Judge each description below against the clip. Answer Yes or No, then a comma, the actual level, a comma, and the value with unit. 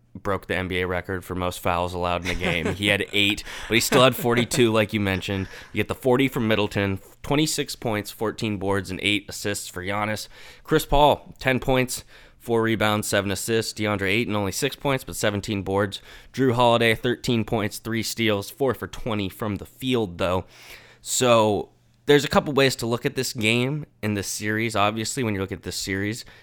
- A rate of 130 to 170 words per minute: No, average, 200 wpm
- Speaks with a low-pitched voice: Yes, low, 105 Hz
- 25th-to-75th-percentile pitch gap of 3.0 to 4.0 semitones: Yes, average, 3.5 semitones